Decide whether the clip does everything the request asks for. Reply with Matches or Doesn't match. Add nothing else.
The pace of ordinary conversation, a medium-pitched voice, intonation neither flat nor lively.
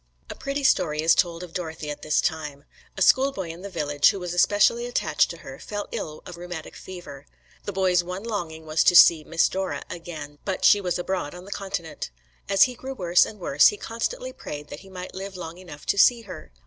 Doesn't match